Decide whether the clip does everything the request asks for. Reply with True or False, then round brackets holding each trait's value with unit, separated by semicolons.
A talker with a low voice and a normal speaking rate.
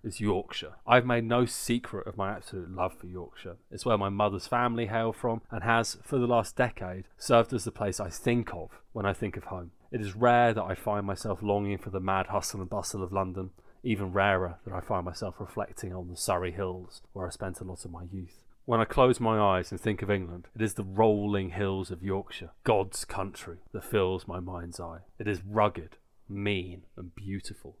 False (100 Hz; 220 wpm)